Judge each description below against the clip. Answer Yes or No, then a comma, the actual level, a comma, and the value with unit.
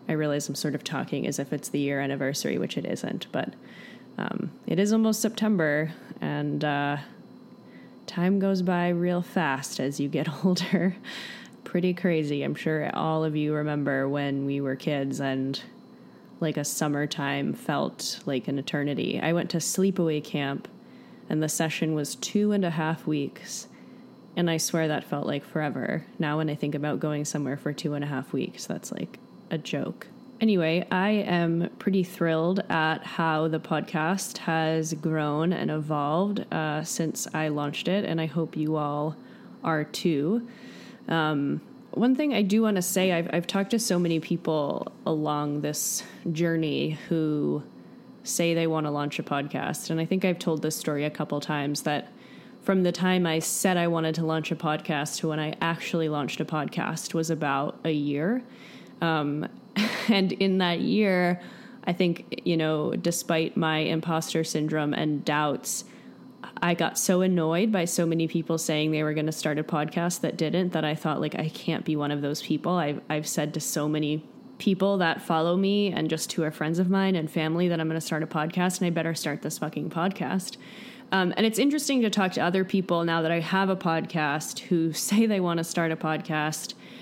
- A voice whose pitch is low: No, medium, 165 Hz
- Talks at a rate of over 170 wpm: Yes, average, 190 wpm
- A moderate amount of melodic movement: Yes, average, 3.6 semitones